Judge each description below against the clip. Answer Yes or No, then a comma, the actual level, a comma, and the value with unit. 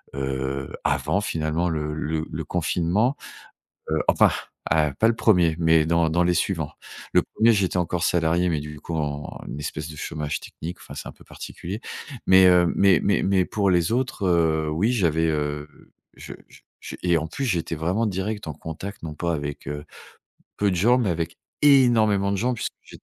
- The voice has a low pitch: Yes, very low, 85 Hz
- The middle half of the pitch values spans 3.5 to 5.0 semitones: Yes, average, 4.1 semitones